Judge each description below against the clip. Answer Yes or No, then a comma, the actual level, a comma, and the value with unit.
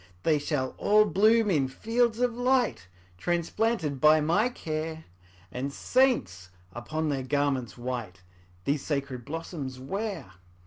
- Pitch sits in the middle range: Yes, medium, 155 Hz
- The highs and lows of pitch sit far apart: Yes, wide, 8.2 semitones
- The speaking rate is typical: No, slow, 125 wpm